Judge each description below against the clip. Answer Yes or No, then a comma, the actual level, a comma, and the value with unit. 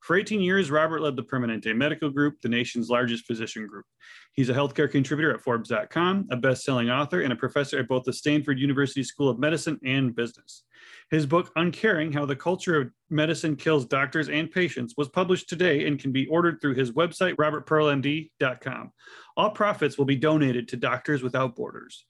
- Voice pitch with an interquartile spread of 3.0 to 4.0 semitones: Yes, average, 3.4 semitones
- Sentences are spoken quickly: No, average, 185 wpm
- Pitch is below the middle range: No, medium, 145 Hz